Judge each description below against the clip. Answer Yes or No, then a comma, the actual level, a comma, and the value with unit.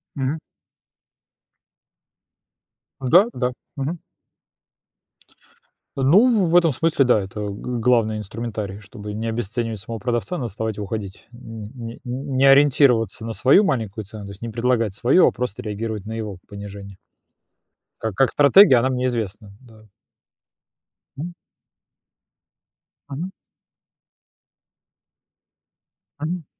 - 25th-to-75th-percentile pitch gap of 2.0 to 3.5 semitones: No, average, 4.2 semitones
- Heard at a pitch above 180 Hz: No, low, 115 Hz